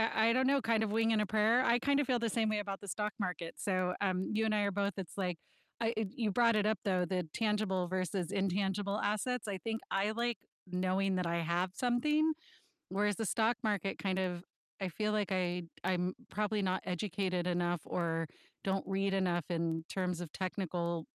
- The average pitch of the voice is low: No, high, 195 Hz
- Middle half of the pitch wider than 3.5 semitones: No, average, 3.0 semitones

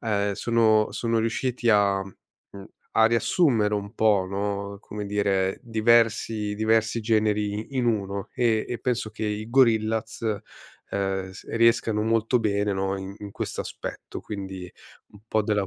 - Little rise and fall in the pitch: Yes, narrow, 2.0 semitones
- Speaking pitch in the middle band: No, low, 105 Hz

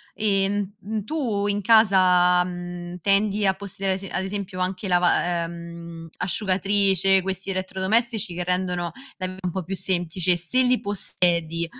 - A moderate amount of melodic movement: No, narrow, 2.2 semitones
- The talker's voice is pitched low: No, high, 190 Hz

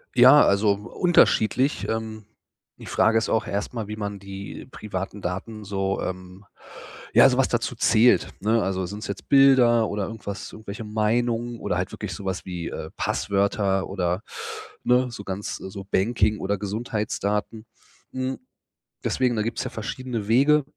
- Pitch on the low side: Yes, low, 105 Hz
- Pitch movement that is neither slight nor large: Yes, average, 3.0 semitones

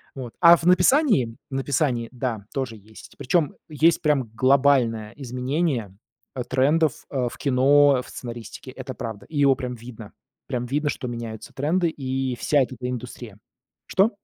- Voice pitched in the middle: No, low, 130 Hz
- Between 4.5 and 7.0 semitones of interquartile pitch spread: No, average, 3.2 semitones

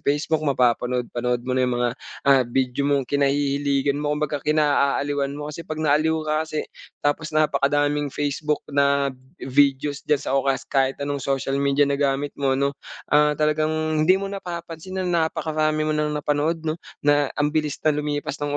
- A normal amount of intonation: No, narrow, 1.7 semitones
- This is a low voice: No, medium, 145 Hz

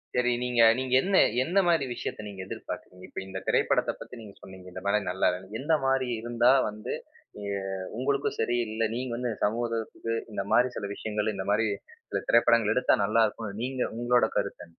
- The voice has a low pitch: Yes, low, 115 Hz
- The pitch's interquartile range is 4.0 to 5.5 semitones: No, average, 3.1 semitones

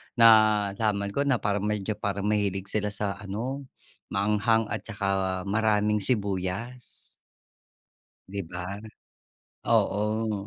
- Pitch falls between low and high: No, low, 105 Hz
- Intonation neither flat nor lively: No, narrow, 1.8 semitones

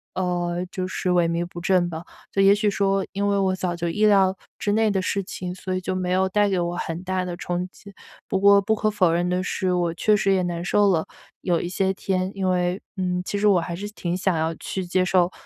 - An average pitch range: No, narrow, 1.9 semitones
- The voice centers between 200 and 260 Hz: No, medium, 185 Hz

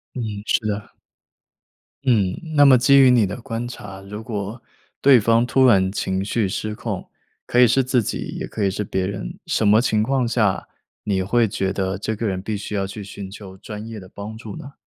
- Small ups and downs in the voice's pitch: No, average, 3.4 semitones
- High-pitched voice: No, low, 105 Hz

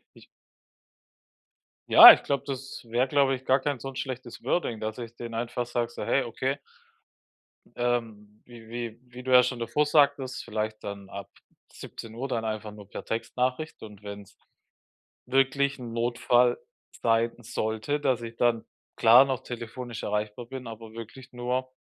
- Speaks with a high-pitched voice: No, low, 120 Hz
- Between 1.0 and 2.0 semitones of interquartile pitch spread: No, narrow, 2.5 semitones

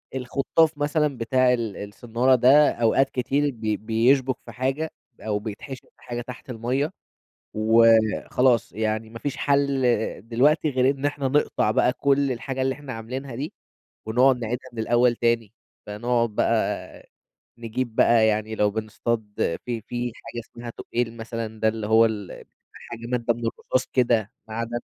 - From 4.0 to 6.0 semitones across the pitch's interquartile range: No, average, 2.9 semitones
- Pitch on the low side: Yes, low, 120 Hz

